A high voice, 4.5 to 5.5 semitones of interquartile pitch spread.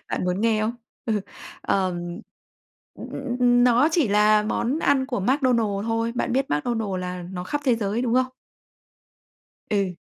No: high, 225 Hz; average, 3.8 semitones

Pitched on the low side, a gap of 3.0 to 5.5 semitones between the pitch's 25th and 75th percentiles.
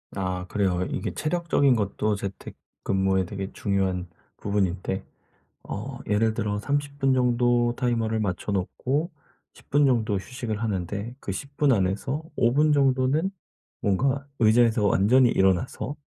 Yes: low, 110 Hz; average, 5.2 semitones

